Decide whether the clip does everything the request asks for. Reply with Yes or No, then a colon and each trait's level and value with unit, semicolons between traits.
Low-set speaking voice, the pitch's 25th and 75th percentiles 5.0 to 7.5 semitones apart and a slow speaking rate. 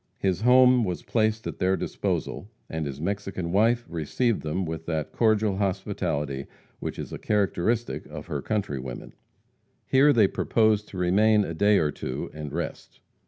No: very low, 95 Hz; average, 5.3 semitones; average, 160 wpm